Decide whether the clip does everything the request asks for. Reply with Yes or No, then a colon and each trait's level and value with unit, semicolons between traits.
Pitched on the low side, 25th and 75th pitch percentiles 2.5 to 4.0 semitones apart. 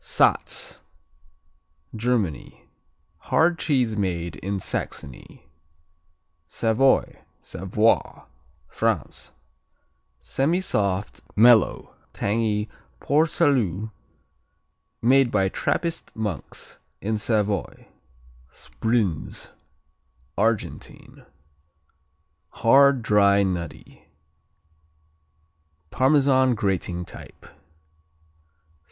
No: low, 110 Hz; average, 4.9 semitones